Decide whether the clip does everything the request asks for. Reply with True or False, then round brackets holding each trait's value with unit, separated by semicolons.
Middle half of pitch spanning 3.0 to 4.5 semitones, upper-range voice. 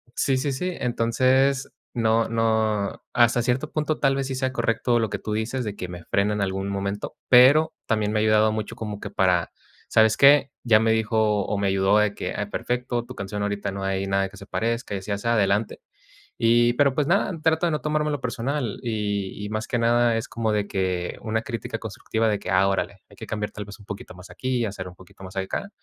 False (3.4 semitones; 110 Hz)